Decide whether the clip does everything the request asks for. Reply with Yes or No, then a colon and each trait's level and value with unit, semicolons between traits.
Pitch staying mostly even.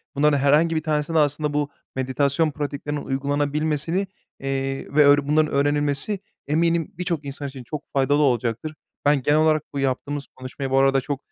Yes: narrow, 1.9 semitones